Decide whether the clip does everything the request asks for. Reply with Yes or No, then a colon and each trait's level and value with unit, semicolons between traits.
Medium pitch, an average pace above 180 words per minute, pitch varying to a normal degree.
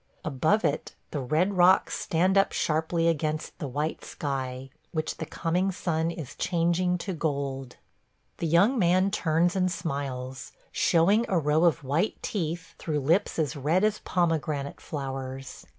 No: medium, 160 Hz; average, 150 wpm; average, 3.9 semitones